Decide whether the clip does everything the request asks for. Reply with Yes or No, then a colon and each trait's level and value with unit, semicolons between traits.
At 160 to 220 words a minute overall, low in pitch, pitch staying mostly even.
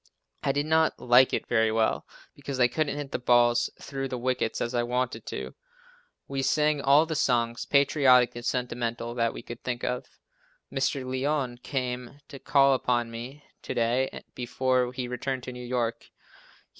Yes: average, 170 wpm; low, 125 Hz; narrow, 2.3 semitones